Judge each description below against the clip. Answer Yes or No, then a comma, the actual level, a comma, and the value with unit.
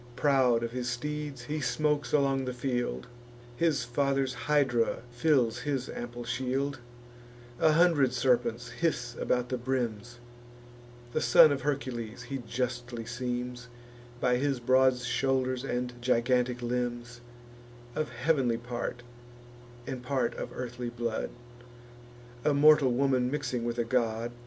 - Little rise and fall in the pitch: Yes, narrow, 2.2 semitones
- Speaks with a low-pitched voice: Yes, low, 125 Hz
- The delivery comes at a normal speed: No, slow, 130 wpm